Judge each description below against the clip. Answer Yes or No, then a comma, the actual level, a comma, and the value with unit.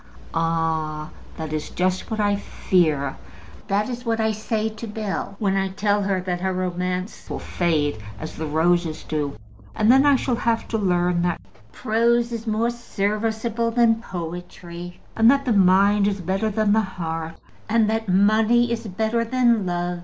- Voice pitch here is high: Yes, high, 200 Hz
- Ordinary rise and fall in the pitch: Yes, average, 4.1 semitones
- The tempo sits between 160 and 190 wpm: Yes, average, 175 wpm